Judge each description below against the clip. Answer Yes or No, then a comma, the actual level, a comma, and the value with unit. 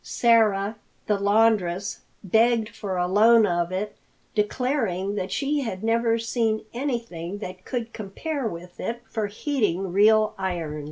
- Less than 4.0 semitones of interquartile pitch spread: Yes, average, 3.5 semitones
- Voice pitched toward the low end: No, high, 215 Hz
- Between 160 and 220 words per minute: No, slow, 135 wpm